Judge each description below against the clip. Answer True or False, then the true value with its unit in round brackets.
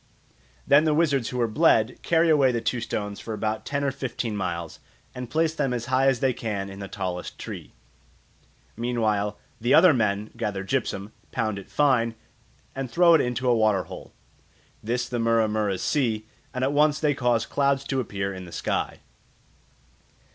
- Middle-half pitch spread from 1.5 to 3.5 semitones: False (4.2 semitones)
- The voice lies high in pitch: False (120 Hz)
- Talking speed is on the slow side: False (180 wpm)